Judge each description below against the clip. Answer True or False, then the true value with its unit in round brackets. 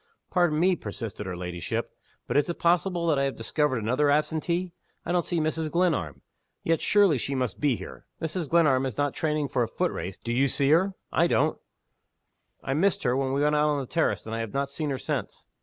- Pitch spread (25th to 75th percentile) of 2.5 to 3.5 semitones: False (4.6 semitones)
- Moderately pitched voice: True (145 Hz)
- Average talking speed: False (225 wpm)